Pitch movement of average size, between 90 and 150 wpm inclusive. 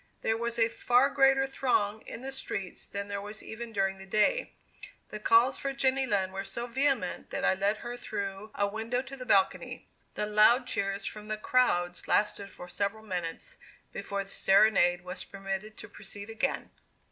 No: average, 3.7 semitones; average, 180 wpm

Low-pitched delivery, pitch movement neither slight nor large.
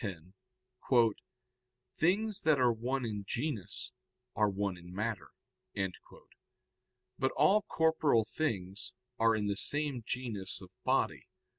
No: low, 115 Hz; wide, 6.6 semitones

